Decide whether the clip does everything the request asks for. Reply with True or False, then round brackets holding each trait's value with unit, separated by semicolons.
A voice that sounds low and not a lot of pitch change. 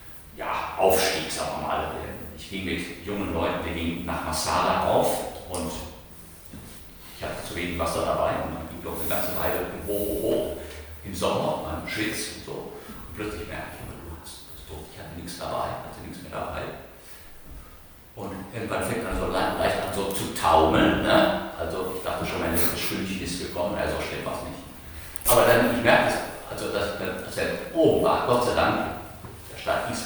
True (85 Hz; 2.3 semitones)